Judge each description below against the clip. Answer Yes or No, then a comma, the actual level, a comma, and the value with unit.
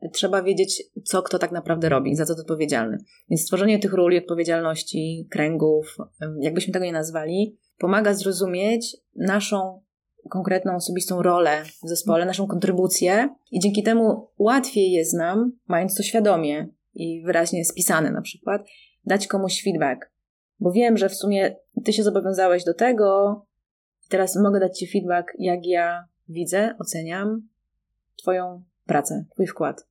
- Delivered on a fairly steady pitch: No, average, 3.0 semitones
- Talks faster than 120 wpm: Yes, average, 140 wpm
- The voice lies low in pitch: No, medium, 185 Hz